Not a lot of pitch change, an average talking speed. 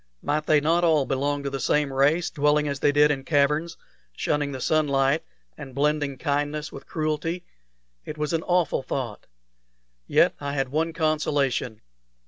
Yes: narrow, 2.0 semitones; average, 160 wpm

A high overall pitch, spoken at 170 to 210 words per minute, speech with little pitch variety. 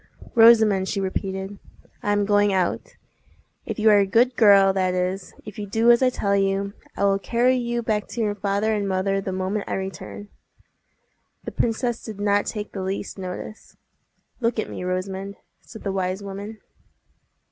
Yes: high, 200 Hz; average, 180 wpm; narrow, 2.1 semitones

